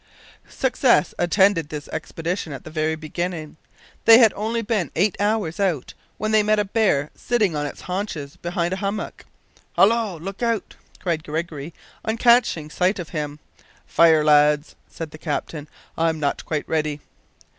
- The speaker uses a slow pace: No, average, 155 wpm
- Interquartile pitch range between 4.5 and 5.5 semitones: Yes, average, 5.2 semitones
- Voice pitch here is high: No, medium, 170 Hz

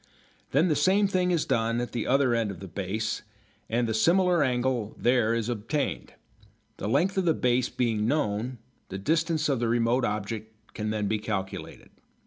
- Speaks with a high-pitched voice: No, low, 120 Hz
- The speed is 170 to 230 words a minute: Yes, average, 180 wpm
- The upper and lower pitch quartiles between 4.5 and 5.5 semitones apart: Yes, average, 5.1 semitones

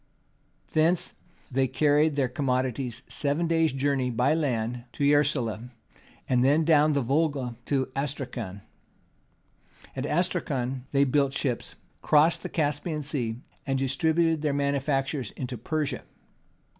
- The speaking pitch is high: No, medium, 140 Hz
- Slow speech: Yes, slow, 120 wpm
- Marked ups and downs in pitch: No, average, 3.0 semitones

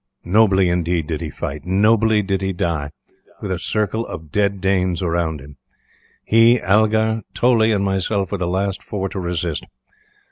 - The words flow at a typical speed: Yes, average, 165 wpm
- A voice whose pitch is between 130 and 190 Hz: No, very low, 95 Hz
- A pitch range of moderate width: Yes, average, 3.5 semitones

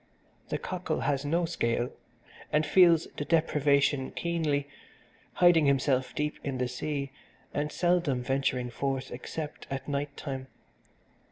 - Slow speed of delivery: Yes, slow, 125 wpm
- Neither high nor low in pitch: Yes, medium, 145 Hz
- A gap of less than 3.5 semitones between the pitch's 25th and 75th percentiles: Yes, average, 3.0 semitones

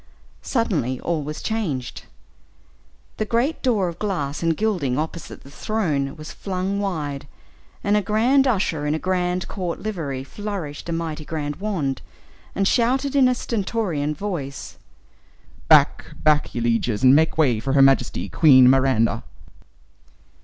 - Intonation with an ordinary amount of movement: No, wide, 6.8 semitones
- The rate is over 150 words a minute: No, average, 145 wpm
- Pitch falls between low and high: Yes, medium, 165 Hz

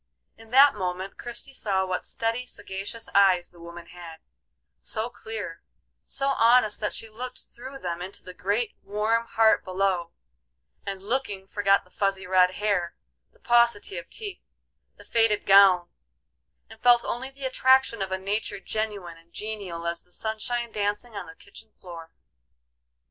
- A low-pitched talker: No, high, 205 Hz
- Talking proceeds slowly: No, average, 155 wpm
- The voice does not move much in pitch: No, average, 3.8 semitones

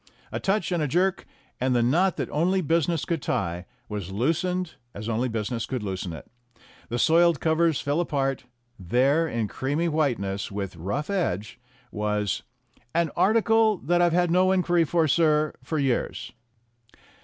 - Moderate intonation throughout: No, wide, 7.2 semitones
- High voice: No, medium, 150 Hz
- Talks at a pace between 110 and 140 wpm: No, average, 155 wpm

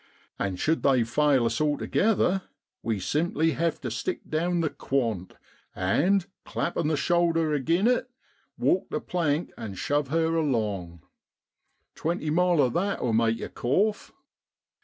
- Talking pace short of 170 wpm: Yes, average, 150 wpm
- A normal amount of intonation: No, wide, 6.4 semitones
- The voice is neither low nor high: Yes, medium, 150 Hz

